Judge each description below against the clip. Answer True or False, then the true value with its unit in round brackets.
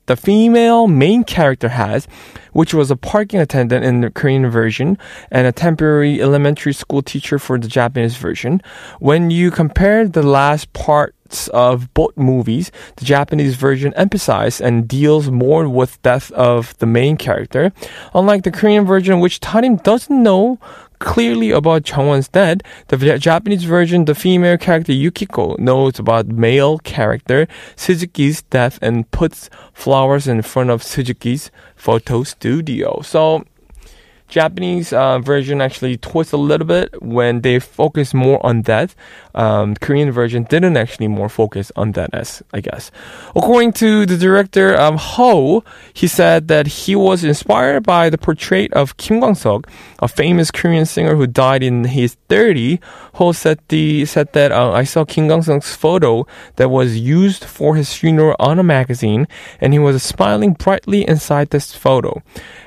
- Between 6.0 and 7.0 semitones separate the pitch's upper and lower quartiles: False (5.4 semitones)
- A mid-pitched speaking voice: True (145 Hz)